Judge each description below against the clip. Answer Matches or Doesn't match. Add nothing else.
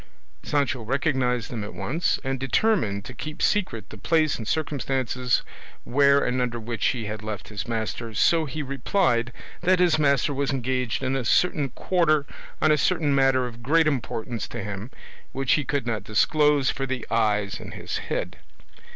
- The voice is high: Doesn't match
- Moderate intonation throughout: Matches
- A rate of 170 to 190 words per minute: Matches